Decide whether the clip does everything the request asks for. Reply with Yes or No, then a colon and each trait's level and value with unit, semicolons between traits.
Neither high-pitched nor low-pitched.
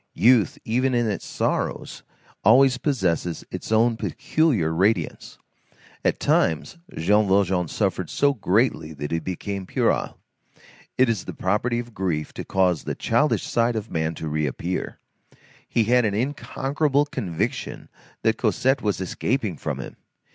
No: low, 105 Hz